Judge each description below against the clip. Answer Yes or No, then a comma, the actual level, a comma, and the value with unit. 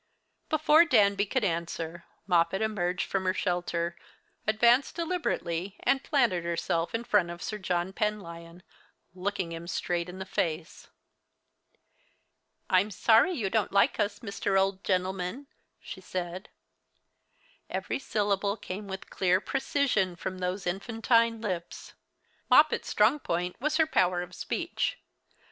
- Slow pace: Yes, slow, 130 wpm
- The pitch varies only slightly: No, average, 3.8 semitones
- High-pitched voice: Yes, high, 195 Hz